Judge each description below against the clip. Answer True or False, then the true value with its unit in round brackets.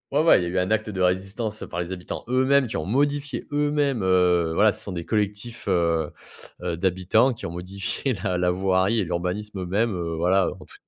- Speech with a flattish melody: False (4.0 semitones)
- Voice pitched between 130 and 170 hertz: False (95 Hz)